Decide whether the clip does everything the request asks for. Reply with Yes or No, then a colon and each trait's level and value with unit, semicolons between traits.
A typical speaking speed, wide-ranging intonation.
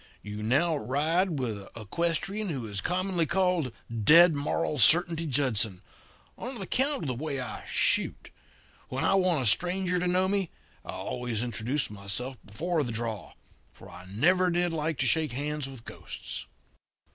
Yes: average, 160 wpm; wide, 6.9 semitones